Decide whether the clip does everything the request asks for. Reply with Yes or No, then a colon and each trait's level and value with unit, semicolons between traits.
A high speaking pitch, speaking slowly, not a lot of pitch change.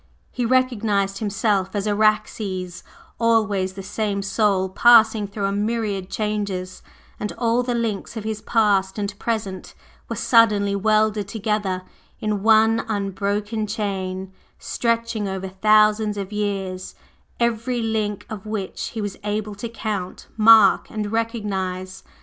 Yes: high, 210 Hz; slow, 130 wpm; narrow, 2.1 semitones